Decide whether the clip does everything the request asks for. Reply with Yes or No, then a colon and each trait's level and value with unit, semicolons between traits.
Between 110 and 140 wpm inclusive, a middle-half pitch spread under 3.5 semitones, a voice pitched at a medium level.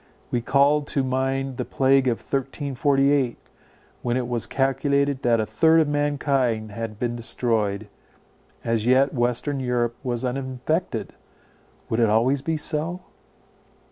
No: slow, 135 wpm; average, 2.9 semitones; low, 130 Hz